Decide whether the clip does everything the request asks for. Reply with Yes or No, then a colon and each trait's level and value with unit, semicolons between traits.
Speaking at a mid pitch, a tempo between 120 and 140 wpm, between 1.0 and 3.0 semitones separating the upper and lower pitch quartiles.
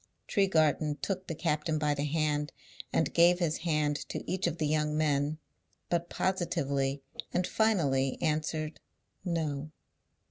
Yes: medium, 155 Hz; slow, 135 wpm; narrow, 2.6 semitones